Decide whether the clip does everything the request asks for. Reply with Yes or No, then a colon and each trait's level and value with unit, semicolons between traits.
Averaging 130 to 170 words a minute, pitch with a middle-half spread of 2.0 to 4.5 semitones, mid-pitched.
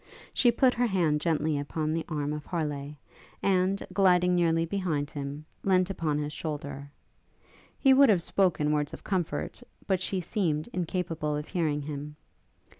Yes: average, 155 wpm; average, 3.8 semitones; medium, 165 Hz